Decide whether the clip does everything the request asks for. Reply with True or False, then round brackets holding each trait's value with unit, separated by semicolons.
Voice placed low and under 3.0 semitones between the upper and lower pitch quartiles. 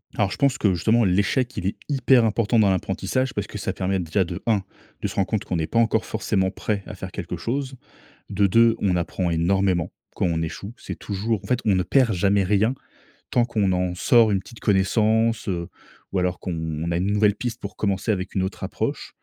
False (100 Hz; 3.5 semitones)